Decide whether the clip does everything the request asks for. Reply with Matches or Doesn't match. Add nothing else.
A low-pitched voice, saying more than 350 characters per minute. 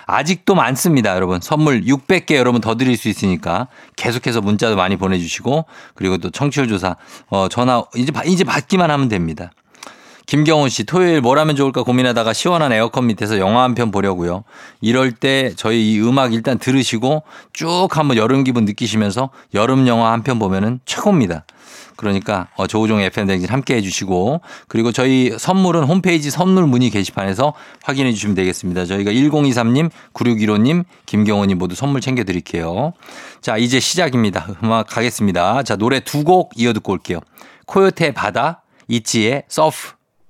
Matches